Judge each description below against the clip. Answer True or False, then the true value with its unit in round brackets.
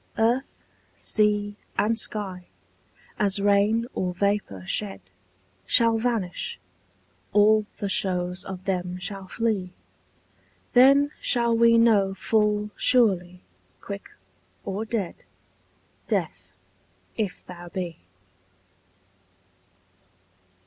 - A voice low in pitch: False (205 Hz)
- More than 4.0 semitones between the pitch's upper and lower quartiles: False (3.5 semitones)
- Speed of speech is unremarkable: False (90 wpm)